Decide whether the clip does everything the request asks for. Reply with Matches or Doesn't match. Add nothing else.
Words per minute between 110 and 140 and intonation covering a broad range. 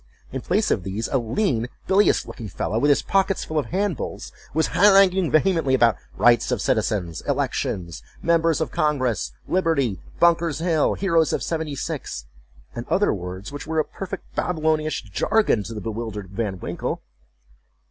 Matches